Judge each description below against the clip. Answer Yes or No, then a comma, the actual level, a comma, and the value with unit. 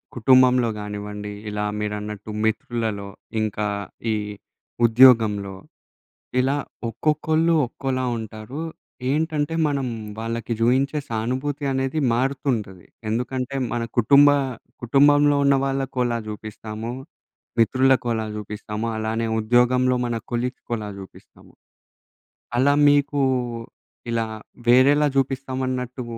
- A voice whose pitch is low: Yes, low, 125 Hz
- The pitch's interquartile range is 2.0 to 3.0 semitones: No, average, 3.6 semitones